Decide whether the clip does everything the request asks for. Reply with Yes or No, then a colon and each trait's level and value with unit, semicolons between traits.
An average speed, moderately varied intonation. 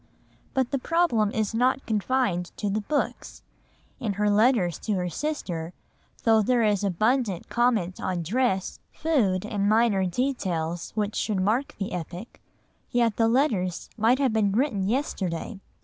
Yes: average, 150 wpm; average, 4.7 semitones